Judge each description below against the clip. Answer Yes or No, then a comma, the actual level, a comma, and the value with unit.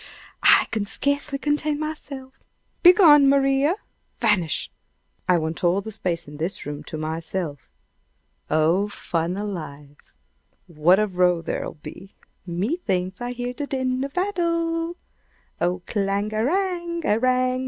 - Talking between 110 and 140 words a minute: Yes, slow, 135 wpm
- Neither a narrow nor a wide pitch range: No, wide, 8.4 semitones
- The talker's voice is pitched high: Yes, high, 215 Hz